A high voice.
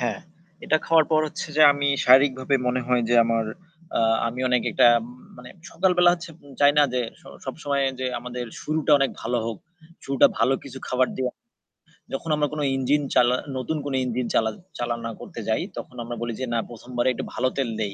No: low, 130 Hz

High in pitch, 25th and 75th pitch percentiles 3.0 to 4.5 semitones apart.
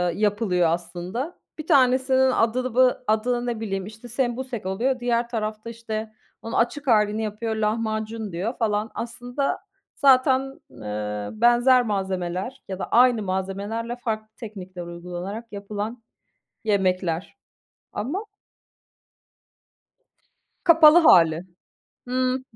Yes: high, 220 Hz; average, 4.2 semitones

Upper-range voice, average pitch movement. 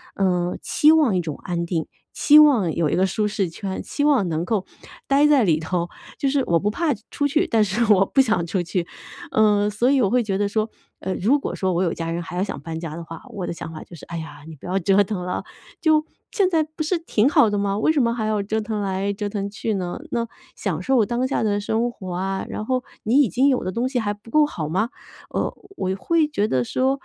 No: high, 205 Hz; wide, 5.9 semitones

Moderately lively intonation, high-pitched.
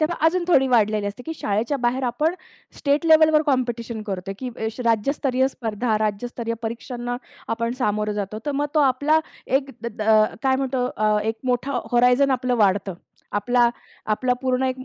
Yes: average, 3.6 semitones; high, 245 Hz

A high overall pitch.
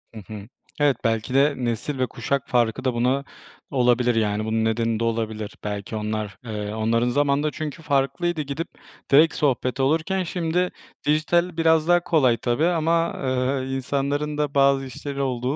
No: low, 135 Hz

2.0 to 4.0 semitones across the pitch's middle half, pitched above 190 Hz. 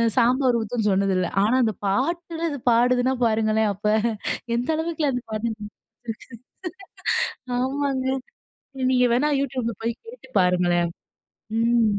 Yes: average, 3.5 semitones; high, 235 Hz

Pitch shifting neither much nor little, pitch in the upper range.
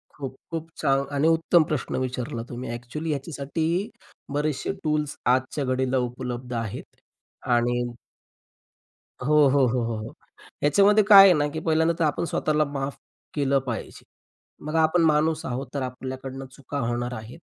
No: average, 3.6 semitones; medium, 140 Hz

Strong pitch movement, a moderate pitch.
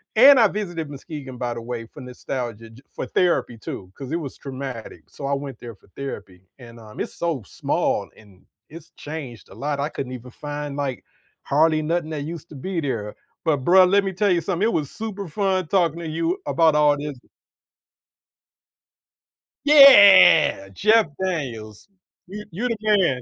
Yes: wide, 6.1 semitones; medium, 150 Hz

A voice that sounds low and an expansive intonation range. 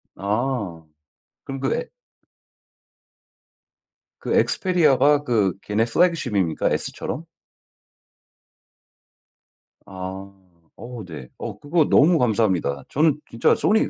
Yes: low, 120 Hz; wide, 7.4 semitones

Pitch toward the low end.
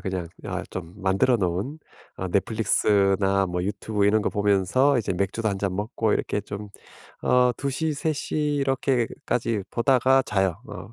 Yes: low, 105 Hz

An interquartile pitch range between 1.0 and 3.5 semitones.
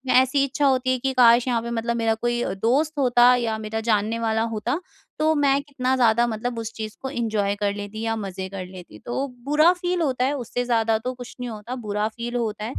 Yes: average, 2.8 semitones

